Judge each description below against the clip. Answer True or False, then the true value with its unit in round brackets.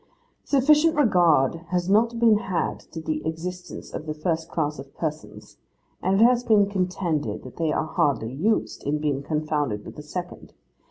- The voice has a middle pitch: True (165 Hz)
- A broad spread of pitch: False (5.0 semitones)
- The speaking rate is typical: True (170 wpm)